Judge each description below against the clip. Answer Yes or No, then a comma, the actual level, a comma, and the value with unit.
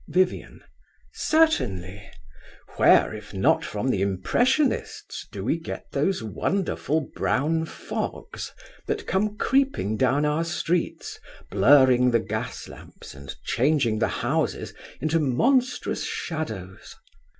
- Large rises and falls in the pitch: Yes, wide, 8.7 semitones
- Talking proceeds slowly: Yes, slow, 110 wpm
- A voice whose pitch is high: No, medium, 140 Hz